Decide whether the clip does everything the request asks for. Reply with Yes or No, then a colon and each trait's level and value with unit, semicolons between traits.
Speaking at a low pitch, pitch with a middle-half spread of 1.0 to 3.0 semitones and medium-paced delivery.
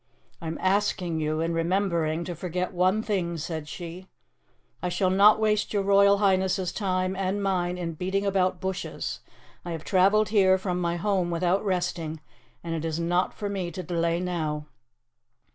No: medium, 180 Hz; narrow, 2.5 semitones; average, 170 wpm